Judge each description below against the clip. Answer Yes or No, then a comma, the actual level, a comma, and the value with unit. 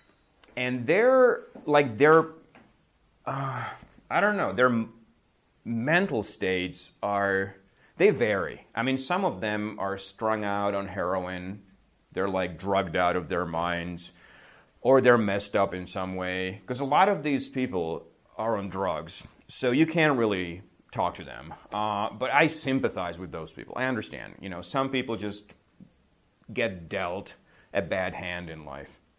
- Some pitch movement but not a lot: No, wide, 5.8 semitones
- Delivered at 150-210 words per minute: Yes, average, 155 wpm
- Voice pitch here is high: No, low, 100 Hz